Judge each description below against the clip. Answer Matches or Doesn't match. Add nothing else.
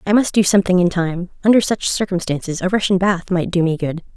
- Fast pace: Matches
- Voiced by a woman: Matches